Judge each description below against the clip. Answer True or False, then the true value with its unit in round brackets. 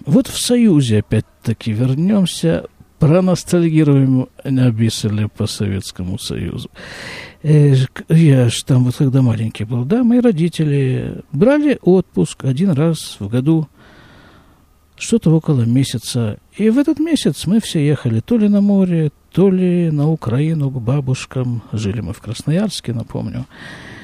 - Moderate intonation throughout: False (6.9 semitones)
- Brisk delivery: False (130 wpm)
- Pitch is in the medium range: True (145 Hz)